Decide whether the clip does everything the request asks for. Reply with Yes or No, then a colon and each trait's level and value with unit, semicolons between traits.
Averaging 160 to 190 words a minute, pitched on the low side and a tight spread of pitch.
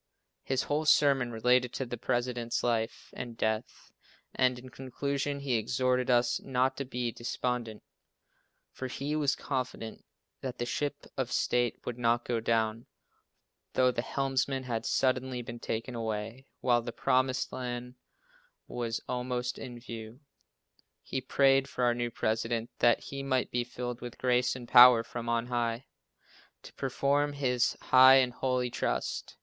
No: average, 150 wpm; low, 125 Hz; narrow, 1.7 semitones